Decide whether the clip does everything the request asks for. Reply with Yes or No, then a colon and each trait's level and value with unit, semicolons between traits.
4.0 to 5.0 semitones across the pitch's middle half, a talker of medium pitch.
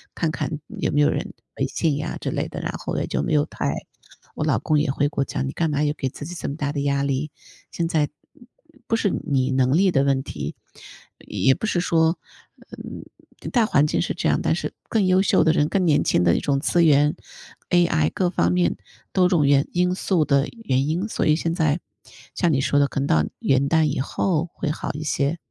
No: average, 3.5 semitones; medium, 150 Hz